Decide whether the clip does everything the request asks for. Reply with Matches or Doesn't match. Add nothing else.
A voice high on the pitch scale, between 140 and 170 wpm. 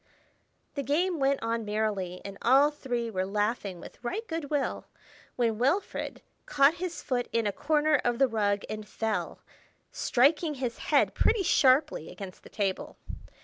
Matches